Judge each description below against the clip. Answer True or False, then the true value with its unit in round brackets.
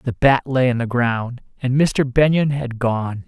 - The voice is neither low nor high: False (125 Hz)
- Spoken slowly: False (200 wpm)